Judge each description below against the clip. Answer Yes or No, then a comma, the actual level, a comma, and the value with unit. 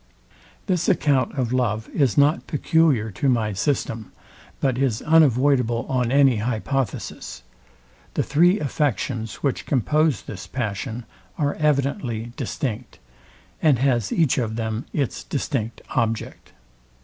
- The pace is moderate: No, slow, 120 wpm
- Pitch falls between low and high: No, low, 130 Hz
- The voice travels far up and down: No, average, 4.3 semitones